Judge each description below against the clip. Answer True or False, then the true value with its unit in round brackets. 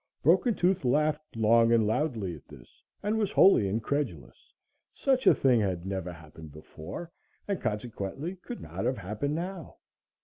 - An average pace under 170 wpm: True (150 wpm)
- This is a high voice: False (120 Hz)